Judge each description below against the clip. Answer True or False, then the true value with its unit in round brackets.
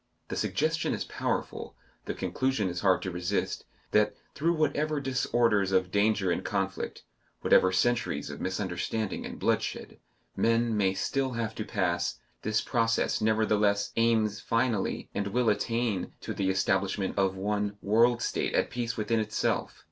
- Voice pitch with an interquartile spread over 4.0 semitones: False (3.3 semitones)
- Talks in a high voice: False (105 Hz)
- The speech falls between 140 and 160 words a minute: True (150 wpm)